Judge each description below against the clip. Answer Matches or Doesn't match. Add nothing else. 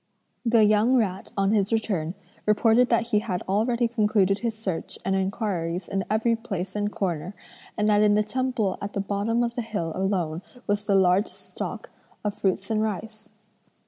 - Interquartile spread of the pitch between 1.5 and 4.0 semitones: Matches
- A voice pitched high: Matches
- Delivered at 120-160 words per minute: Doesn't match